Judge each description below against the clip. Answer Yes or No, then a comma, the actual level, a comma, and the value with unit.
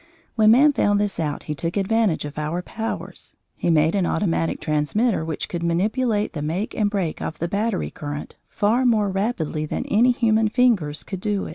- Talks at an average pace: Yes, average, 185 wpm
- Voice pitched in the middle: No, high, 200 Hz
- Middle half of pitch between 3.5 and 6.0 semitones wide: Yes, wide, 5.4 semitones